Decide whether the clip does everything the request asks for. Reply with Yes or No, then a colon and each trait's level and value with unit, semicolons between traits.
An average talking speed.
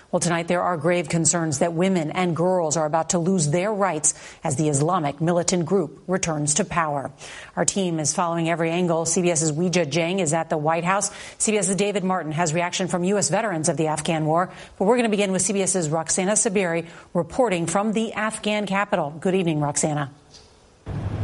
Yes: average, 190 wpm